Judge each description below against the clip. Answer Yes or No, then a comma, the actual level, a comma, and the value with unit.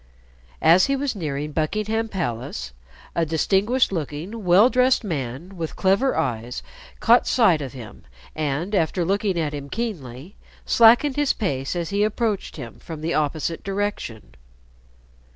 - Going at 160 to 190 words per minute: No, average, 140 wpm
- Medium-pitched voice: Yes, medium, 175 Hz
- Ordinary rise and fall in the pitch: No, wide, 6.6 semitones